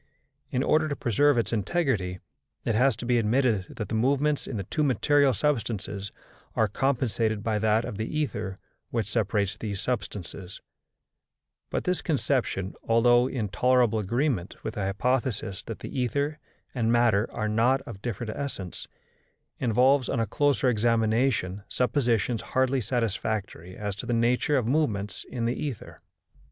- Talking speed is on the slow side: No, average, 150 wpm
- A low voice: Yes, low, 115 Hz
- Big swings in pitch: No, average, 4.0 semitones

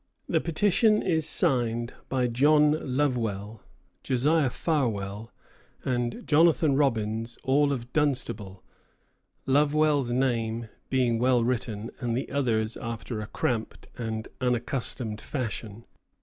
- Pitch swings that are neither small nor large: Yes, average, 3.9 semitones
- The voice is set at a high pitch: No, low, 125 Hz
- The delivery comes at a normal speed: No, slow, 105 wpm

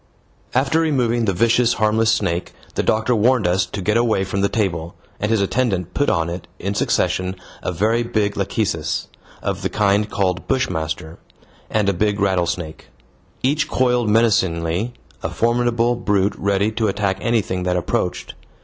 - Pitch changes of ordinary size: Yes, average, 4.1 semitones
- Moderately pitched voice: No, low, 105 Hz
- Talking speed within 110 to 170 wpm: Yes, average, 160 wpm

